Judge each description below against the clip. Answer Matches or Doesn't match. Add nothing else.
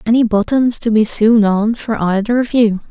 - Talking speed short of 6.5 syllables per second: Matches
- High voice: Matches